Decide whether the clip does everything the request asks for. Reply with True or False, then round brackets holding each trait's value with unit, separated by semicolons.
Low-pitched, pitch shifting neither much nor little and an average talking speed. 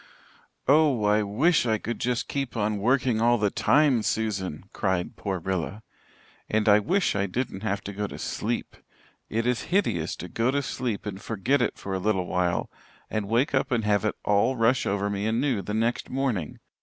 True (110 Hz; 3.8 semitones; 195 wpm)